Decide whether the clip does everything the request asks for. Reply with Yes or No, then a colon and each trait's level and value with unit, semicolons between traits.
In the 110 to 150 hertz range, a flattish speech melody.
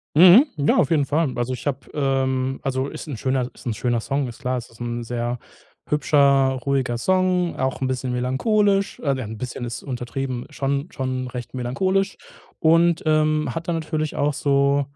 No: low, 135 Hz; average, 3.4 semitones